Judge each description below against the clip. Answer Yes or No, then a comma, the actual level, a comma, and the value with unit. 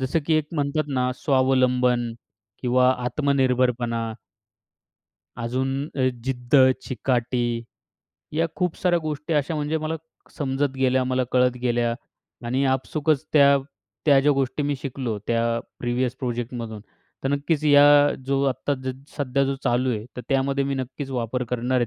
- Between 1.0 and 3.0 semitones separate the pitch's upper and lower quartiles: Yes, narrow, 2.4 semitones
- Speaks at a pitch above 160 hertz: No, low, 130 Hz